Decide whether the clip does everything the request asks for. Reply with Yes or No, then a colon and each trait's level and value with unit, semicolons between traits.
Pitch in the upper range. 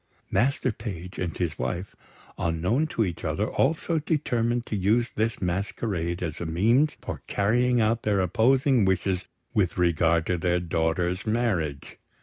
No: low, 100 Hz